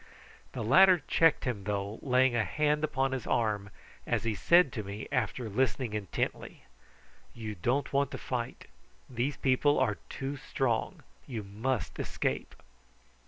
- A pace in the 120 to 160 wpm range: Yes, average, 145 wpm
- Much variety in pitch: No, average, 4.3 semitones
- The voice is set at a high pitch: No, low, 125 Hz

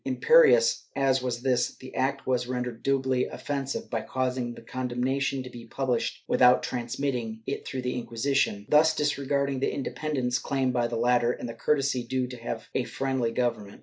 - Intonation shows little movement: Yes, narrow, 2.1 semitones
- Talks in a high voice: No, low, 130 Hz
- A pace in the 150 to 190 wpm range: Yes, average, 175 wpm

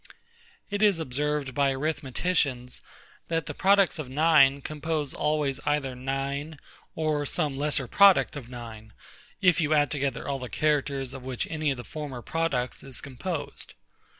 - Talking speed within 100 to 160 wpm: Yes, average, 150 wpm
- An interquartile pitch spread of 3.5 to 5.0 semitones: No, average, 2.7 semitones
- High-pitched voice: No, medium, 145 Hz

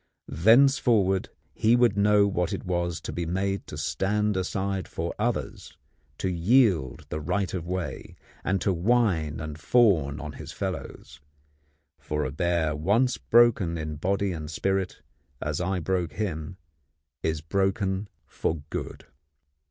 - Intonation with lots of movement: No, average, 4.2 semitones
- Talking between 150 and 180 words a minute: No, average, 140 wpm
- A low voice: Yes, very low, 95 Hz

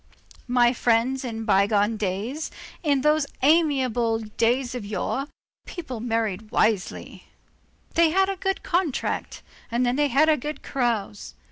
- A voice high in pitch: Yes, high, 245 Hz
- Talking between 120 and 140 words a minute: Yes, slow, 135 wpm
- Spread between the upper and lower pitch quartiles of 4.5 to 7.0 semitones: Yes, average, 4.8 semitones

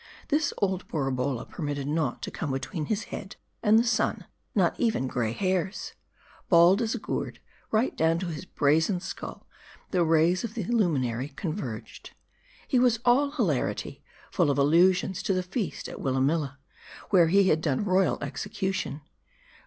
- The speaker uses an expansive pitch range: Yes, wide, 5.8 semitones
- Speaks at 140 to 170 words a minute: Yes, average, 160 wpm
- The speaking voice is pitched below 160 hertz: No, medium, 175 Hz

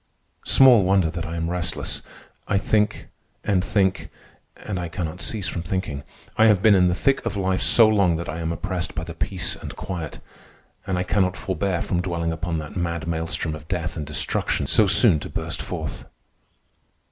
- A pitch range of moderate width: Yes, average, 3.1 semitones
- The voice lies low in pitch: Yes, very low, 90 Hz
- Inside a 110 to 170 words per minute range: No, average, 190 wpm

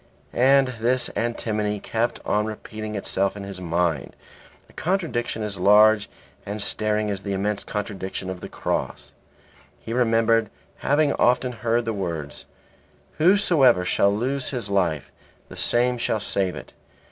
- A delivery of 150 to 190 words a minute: No, average, 140 wpm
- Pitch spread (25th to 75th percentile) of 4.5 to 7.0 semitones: No, average, 3.4 semitones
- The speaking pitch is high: No, low, 110 Hz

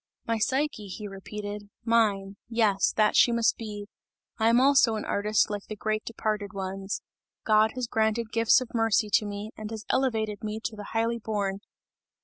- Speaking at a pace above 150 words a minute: Yes, average, 175 wpm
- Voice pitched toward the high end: Yes, high, 215 Hz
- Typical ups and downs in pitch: No, narrow, 1.8 semitones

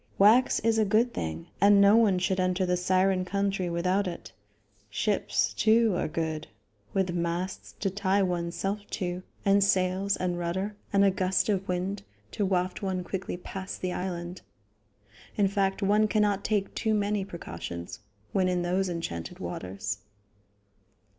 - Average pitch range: No, narrow, 2.1 semitones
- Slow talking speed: No, average, 155 wpm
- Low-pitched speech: No, high, 190 Hz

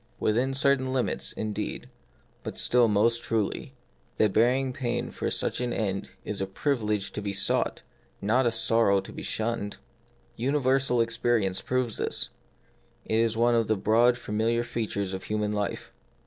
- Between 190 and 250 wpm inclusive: No, average, 160 wpm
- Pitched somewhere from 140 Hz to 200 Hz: No, low, 115 Hz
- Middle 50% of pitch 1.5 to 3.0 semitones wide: Yes, average, 2.7 semitones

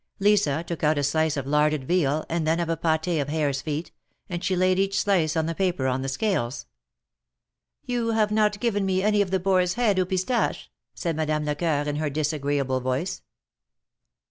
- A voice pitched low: No, medium, 165 Hz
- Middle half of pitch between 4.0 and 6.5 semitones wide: Yes, average, 4.5 semitones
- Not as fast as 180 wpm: No, average, 195 wpm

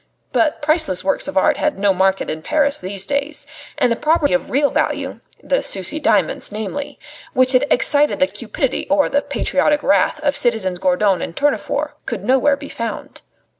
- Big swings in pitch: Yes, wide, 6.7 semitones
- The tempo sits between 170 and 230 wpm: Yes, average, 175 wpm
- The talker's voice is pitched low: No, very high, 270 Hz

